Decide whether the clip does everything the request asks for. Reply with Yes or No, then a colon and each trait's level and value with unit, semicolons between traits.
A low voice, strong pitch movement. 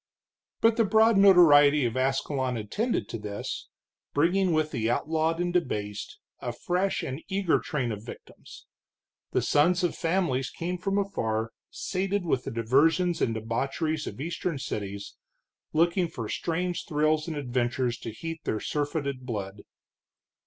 No: medium, 150 Hz; wide, 6.6 semitones